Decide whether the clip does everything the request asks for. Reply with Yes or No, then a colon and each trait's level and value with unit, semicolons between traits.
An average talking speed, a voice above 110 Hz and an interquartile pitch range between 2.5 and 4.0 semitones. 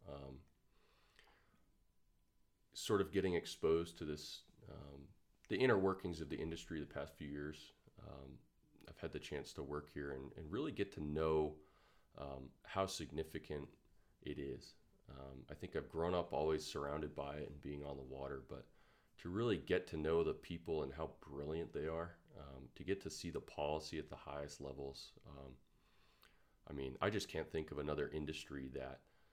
No: average, 180 wpm; very low, 75 Hz; average, 2.8 semitones